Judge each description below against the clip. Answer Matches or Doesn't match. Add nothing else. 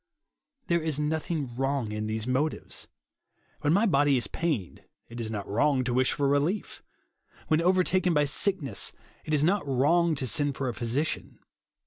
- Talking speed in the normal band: Matches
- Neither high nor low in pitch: Matches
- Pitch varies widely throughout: Doesn't match